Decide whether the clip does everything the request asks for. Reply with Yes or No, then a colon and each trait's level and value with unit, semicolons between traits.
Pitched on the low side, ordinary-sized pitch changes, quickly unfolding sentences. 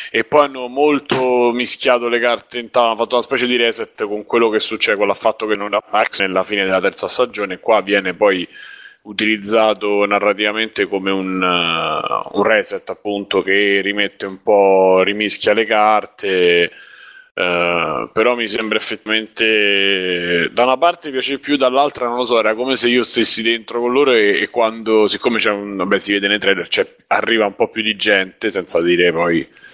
Yes: low, 110 Hz; average, 3.4 semitones; fast, 180 wpm